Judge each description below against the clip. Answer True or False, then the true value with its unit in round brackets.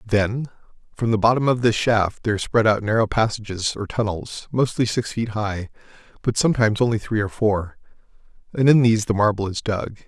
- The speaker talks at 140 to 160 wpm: False (185 wpm)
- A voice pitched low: True (110 Hz)